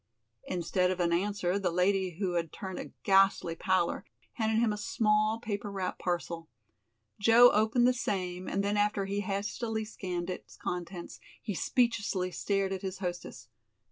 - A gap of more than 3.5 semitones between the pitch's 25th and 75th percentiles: No, average, 2.8 semitones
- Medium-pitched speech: No, high, 195 Hz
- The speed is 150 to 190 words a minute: Yes, average, 160 wpm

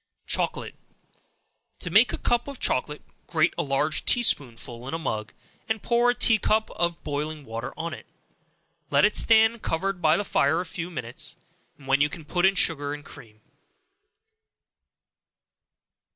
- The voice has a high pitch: No, medium, 165 Hz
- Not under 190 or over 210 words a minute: No, average, 160 wpm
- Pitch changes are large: Yes, wide, 6.2 semitones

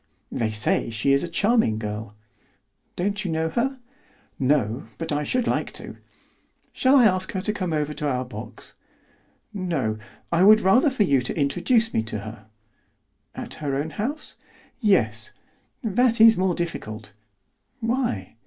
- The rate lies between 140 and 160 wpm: Yes, average, 155 wpm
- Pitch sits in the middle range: Yes, medium, 165 Hz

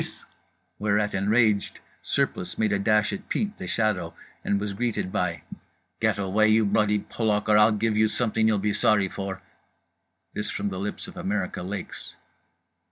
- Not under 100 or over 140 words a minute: No, average, 165 wpm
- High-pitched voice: No, low, 105 Hz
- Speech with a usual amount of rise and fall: No, narrow, 1.6 semitones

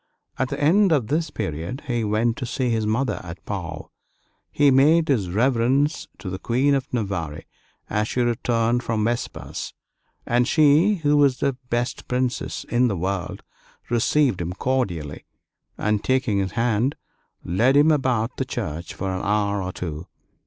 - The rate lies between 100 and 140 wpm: No, average, 160 wpm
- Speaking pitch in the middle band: No, low, 120 Hz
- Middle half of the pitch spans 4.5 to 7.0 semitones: Yes, average, 5.1 semitones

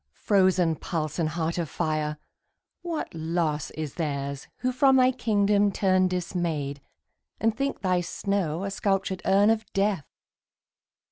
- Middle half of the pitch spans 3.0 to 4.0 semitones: No, average, 4.4 semitones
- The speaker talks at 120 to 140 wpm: Yes, slow, 135 wpm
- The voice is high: No, medium, 180 Hz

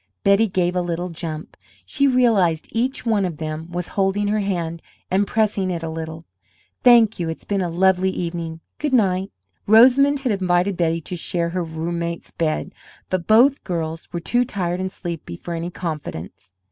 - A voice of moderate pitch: Yes, medium, 180 Hz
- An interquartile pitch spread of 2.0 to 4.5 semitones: Yes, average, 3.5 semitones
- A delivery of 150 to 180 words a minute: Yes, average, 170 wpm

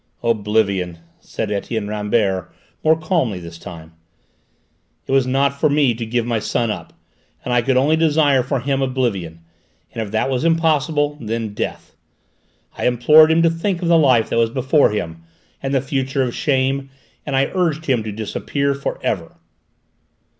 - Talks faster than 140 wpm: Yes, average, 170 wpm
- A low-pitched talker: Yes, low, 130 Hz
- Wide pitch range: No, average, 5.0 semitones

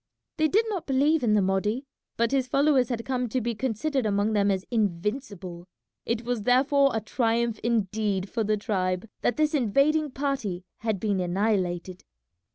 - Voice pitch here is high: Yes, high, 225 Hz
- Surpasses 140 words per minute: Yes, average, 165 wpm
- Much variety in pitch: No, average, 4.8 semitones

